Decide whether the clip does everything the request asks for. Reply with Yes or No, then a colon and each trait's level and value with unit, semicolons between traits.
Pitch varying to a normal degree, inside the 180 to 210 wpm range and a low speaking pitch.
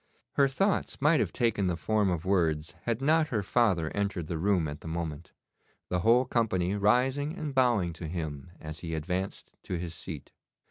No: wide, 6.6 semitones; average, 185 wpm; very low, 95 Hz